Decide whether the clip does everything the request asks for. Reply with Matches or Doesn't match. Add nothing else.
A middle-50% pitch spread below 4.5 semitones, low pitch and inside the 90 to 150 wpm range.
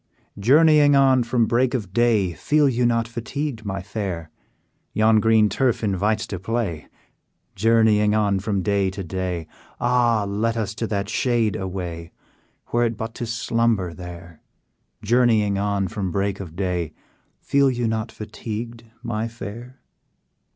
Matches